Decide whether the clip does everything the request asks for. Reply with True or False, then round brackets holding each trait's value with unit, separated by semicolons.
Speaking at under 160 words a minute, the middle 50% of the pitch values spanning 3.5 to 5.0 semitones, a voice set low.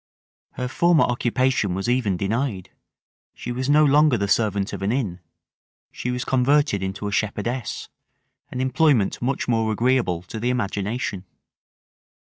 True (140 wpm; 4.5 semitones; 120 Hz)